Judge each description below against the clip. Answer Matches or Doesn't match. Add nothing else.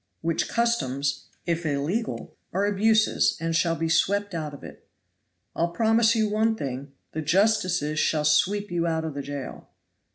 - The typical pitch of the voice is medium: Matches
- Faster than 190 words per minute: Doesn't match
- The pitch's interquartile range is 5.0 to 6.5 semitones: Matches